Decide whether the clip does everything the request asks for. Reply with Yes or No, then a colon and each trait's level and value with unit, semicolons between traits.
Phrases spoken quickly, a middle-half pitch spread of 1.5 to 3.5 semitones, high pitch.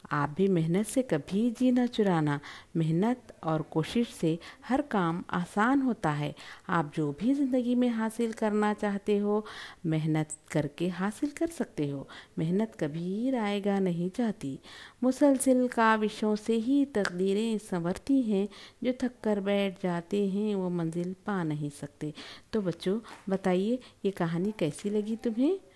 No: fast, 145 wpm; wide, 5.5 semitones; high, 200 Hz